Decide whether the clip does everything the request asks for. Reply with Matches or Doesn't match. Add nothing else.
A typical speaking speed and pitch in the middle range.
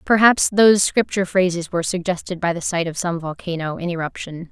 Matches